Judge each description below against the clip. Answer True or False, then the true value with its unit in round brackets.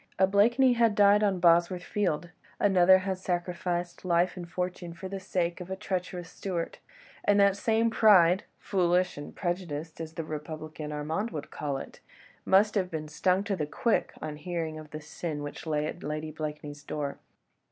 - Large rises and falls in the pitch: False (3.5 semitones)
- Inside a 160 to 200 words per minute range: True (170 wpm)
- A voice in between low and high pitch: True (175 Hz)